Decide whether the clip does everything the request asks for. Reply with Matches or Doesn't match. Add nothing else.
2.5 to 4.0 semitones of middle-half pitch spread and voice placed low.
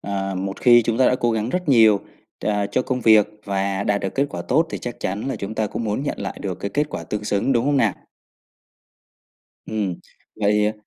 Matches